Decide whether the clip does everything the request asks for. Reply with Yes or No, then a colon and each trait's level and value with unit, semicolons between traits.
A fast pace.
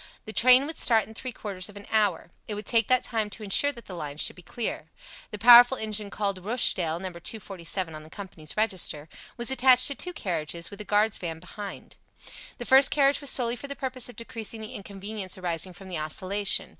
Yes: fast, 215 wpm